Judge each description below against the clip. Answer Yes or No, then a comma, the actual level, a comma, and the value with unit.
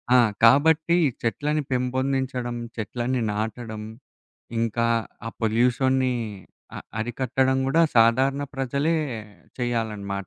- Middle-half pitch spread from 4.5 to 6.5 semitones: No, average, 2.7 semitones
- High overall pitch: No, low, 125 Hz